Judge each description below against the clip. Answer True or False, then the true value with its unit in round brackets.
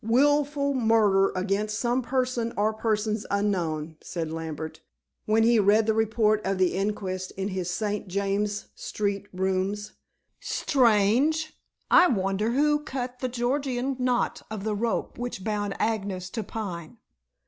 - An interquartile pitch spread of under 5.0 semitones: True (3.7 semitones)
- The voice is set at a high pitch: True (215 Hz)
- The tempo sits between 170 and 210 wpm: False (135 wpm)